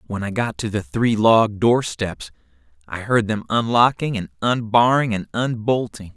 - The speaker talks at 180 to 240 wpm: No, average, 155 wpm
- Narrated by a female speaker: No, male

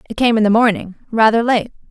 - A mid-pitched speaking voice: No, high, 220 Hz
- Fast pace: Yes, fast, 220 wpm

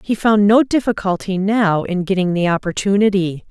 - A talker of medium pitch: No, high, 195 Hz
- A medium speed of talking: Yes, average, 155 wpm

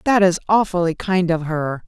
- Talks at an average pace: Yes, average, 190 wpm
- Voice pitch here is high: No, medium, 180 Hz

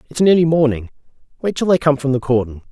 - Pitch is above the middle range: No, medium, 140 Hz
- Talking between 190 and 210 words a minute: No, fast, 220 wpm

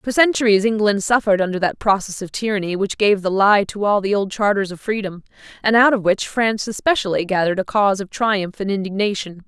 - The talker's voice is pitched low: No, high, 205 Hz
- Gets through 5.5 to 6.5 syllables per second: Yes, 6.0 syllables/s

